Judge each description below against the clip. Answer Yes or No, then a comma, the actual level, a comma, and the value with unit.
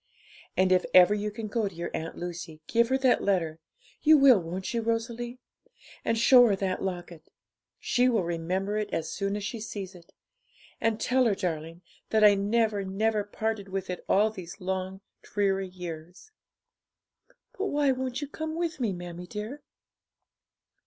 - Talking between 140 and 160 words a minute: No, average, 170 wpm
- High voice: Yes, high, 200 Hz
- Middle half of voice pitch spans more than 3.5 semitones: Yes, average, 4.2 semitones